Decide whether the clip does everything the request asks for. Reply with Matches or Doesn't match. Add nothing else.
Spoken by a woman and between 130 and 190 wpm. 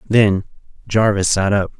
Doesn't match